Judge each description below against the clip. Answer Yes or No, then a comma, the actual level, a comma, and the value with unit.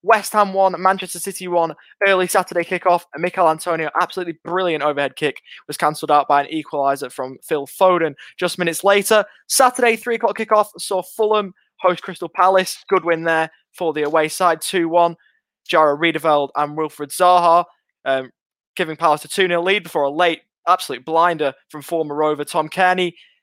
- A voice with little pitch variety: No, average, 3.2 semitones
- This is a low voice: No, medium, 175 Hz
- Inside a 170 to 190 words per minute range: Yes, average, 175 wpm